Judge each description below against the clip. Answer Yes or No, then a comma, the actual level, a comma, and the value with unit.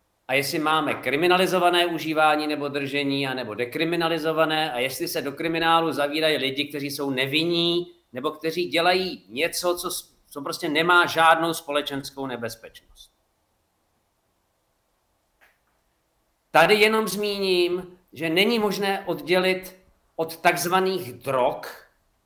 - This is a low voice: No, medium, 165 Hz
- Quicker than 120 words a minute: No, slow, 110 wpm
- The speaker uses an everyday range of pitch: Yes, average, 3.4 semitones